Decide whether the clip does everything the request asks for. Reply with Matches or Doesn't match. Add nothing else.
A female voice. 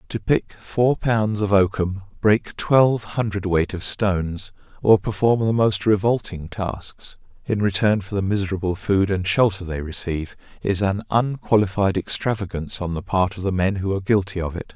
Doesn't match